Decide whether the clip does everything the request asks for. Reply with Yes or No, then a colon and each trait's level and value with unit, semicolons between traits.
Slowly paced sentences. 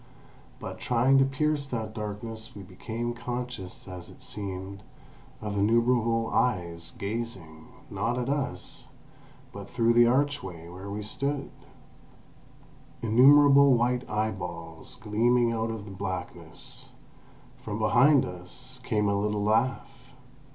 Yes: slow, 115 wpm